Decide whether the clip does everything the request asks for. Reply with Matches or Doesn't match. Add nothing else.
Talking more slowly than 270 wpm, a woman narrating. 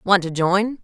Matches